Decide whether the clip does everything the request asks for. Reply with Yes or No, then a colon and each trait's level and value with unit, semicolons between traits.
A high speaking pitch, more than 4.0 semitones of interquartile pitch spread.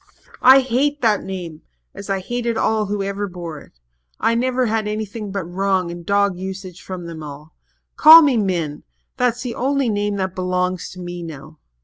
Yes: high, 195 Hz; average, 4.5 semitones